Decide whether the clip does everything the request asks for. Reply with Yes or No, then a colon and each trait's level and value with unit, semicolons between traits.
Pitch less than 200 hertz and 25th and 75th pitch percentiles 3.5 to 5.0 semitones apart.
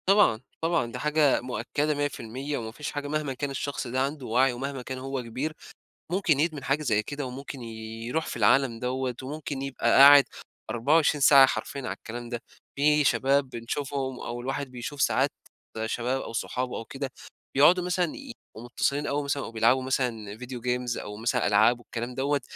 No: low, 135 Hz; average, 3.1 semitones